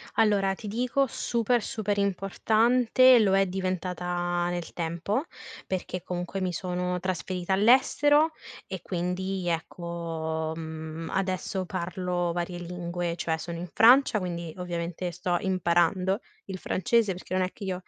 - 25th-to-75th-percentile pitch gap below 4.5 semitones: Yes, narrow, 2.4 semitones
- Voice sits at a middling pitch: Yes, medium, 180 Hz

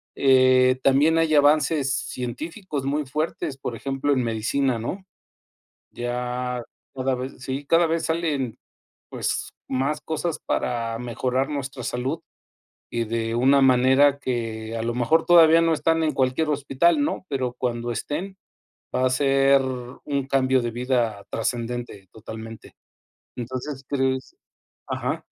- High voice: No, low, 130 Hz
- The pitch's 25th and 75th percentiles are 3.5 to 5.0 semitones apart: No, average, 2.9 semitones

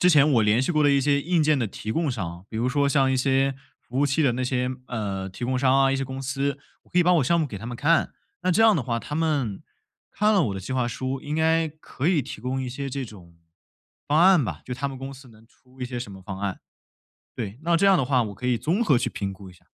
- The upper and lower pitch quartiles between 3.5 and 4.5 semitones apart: Yes, average, 4.0 semitones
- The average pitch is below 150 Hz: Yes, low, 135 Hz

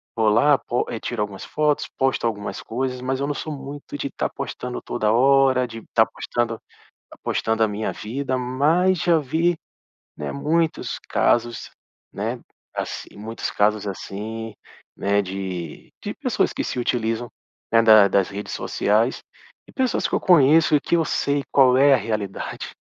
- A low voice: Yes, low, 120 Hz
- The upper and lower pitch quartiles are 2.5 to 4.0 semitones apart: No, average, 4.7 semitones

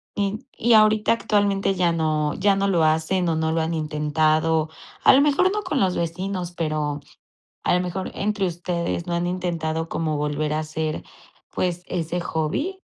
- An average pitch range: Yes, average, 3.6 semitones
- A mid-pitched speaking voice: Yes, medium, 170 Hz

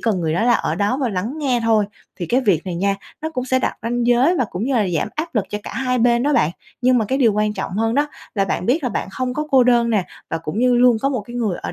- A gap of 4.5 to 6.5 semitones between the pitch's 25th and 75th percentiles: No, average, 3.9 semitones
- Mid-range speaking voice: No, high, 235 Hz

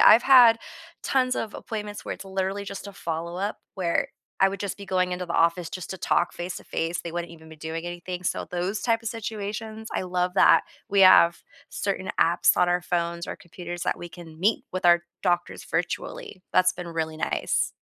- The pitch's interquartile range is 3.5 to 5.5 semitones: No, average, 2.8 semitones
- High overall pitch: No, medium, 180 Hz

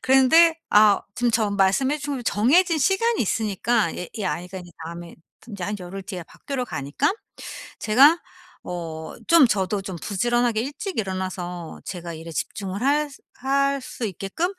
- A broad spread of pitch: Yes, wide, 6.9 semitones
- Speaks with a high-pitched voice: Yes, high, 215 Hz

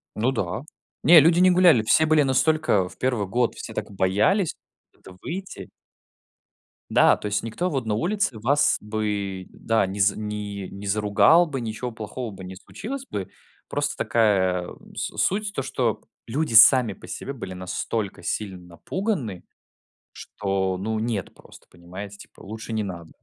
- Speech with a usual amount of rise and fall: No, wide, 5.7 semitones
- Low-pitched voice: Yes, low, 110 Hz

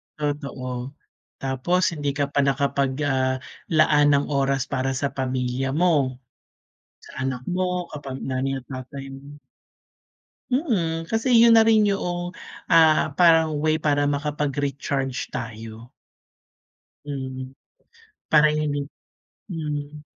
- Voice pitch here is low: No, medium, 145 Hz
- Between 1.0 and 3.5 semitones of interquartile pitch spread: Yes, average, 3.1 semitones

